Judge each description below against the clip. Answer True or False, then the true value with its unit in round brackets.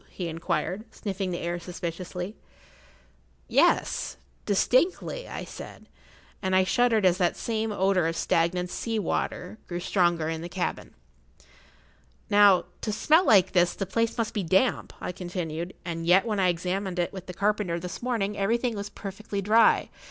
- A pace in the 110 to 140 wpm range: False (155 wpm)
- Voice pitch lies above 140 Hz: True (190 Hz)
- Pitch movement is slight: False (3.2 semitones)